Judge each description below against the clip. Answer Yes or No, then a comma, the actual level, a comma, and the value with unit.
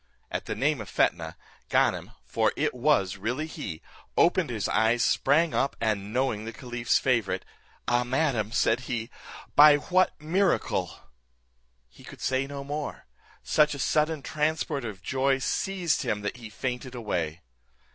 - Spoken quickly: No, average, 150 wpm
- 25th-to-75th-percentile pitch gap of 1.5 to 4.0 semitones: No, average, 5.2 semitones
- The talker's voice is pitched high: No, low, 130 Hz